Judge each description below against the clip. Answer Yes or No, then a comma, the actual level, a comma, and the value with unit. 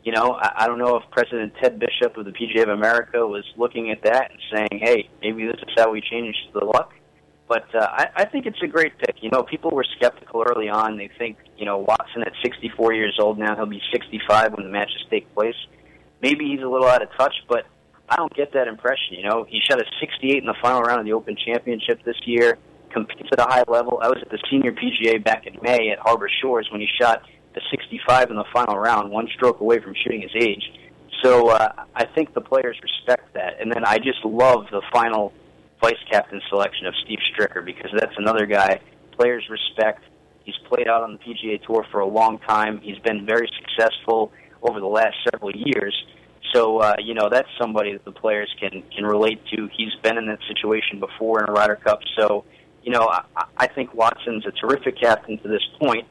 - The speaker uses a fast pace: Yes, fast, 220 wpm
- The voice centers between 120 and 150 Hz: No, low, 110 Hz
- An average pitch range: No, narrow, 2.3 semitones